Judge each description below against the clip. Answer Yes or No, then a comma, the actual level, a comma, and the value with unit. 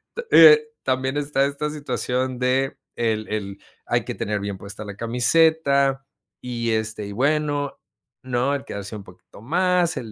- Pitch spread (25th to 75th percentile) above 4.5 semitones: Yes, average, 4.9 semitones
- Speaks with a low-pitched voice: Yes, low, 130 Hz